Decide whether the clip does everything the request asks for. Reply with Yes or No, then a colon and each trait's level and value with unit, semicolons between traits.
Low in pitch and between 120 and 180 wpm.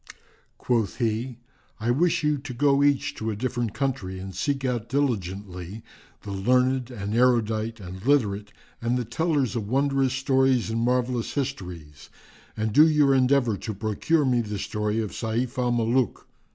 Yes: low, 120 Hz; average, 160 wpm